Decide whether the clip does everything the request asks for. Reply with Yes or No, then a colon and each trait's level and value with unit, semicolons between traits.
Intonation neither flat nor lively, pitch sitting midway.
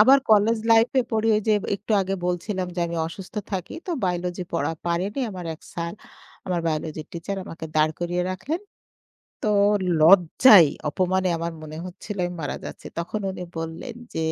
Yes: average, 3.6 semitones; medium, 180 Hz